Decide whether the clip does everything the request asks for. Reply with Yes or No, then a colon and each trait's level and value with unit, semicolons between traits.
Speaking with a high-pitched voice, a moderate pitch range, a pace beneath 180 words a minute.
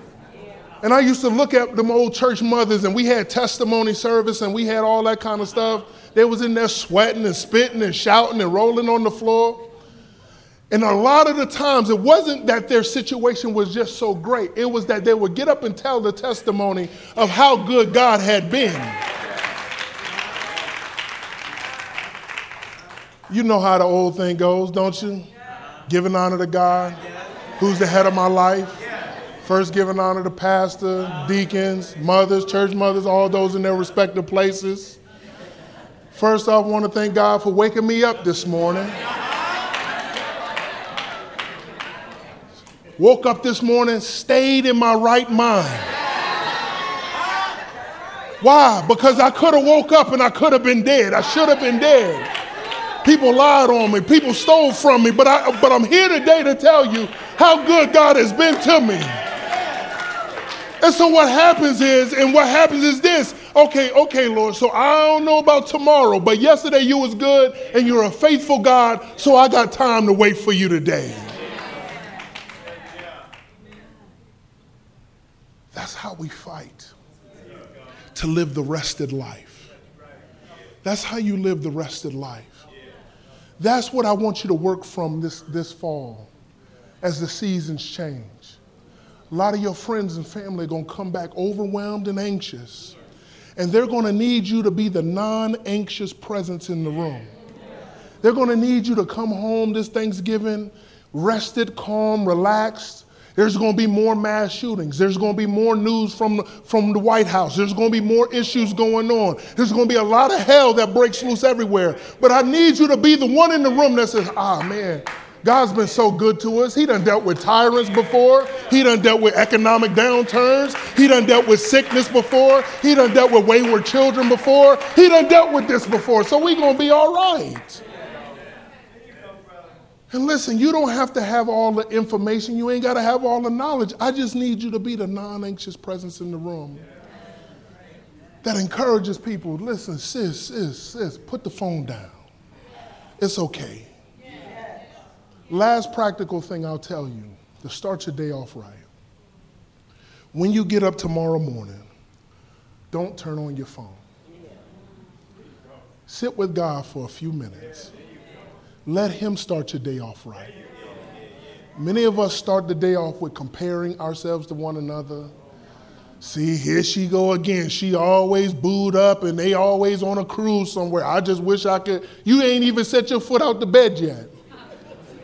Yes: high, 215 Hz; average, 5.0 semitones; average, 170 wpm